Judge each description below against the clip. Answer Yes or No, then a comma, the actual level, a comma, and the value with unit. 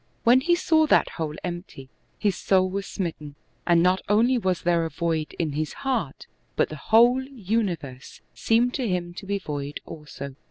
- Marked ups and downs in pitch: Yes, wide, 6.4 semitones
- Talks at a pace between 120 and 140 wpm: No, average, 185 wpm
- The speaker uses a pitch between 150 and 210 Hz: Yes, medium, 185 Hz